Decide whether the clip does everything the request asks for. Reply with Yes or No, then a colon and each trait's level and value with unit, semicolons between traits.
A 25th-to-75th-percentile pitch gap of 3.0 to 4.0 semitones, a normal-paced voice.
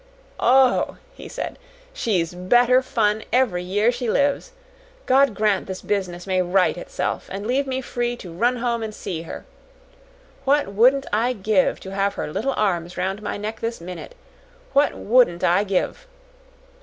No: average, 5.0 semitones; average, 160 wpm